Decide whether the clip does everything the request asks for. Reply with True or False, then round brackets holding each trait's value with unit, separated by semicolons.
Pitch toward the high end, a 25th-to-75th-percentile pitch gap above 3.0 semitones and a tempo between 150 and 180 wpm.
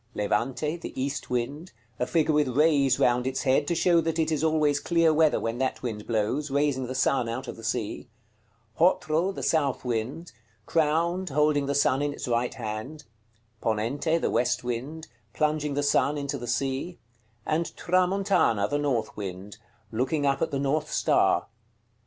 False (140 Hz; 4.2 semitones; 170 wpm)